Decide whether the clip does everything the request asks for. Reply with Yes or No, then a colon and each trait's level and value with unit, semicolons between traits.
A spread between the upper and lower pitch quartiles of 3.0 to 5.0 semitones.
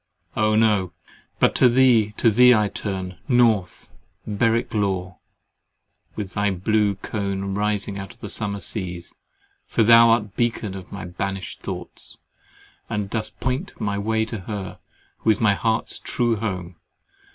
No: narrow, 2.6 semitones